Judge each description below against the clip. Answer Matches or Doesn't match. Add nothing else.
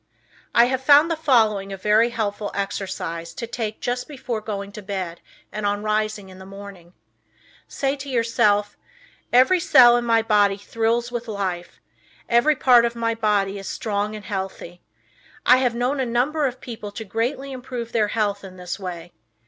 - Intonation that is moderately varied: Matches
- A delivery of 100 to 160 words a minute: Doesn't match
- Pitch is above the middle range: Matches